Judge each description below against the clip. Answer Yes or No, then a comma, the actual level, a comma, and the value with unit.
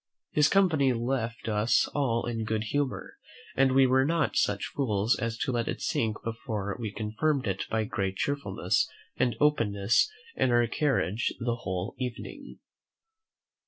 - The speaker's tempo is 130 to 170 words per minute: Yes, average, 150 wpm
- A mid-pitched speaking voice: No, low, 115 Hz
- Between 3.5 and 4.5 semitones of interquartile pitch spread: Yes, average, 4.0 semitones